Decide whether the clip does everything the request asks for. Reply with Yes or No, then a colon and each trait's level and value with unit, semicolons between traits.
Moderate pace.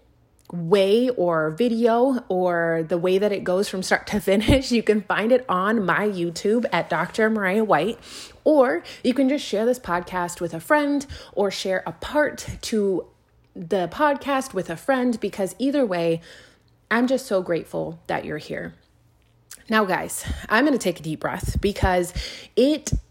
Yes: average, 170 wpm